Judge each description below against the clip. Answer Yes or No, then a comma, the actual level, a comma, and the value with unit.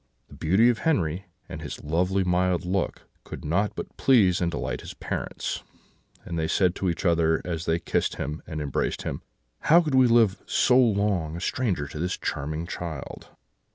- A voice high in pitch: No, very low, 90 Hz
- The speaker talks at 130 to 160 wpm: No, average, 185 wpm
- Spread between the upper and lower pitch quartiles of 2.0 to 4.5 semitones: Yes, average, 3.8 semitones